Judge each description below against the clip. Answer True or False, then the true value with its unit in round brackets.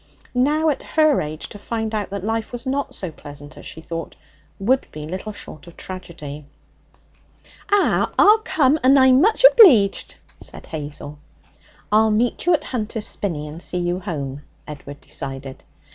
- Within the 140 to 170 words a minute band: True (160 wpm)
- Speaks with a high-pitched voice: True (200 Hz)